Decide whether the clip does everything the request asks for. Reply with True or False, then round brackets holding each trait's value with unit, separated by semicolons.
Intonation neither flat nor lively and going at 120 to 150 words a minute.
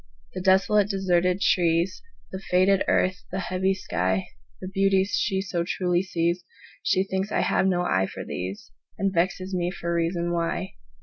False (1.9 semitones; 140 wpm)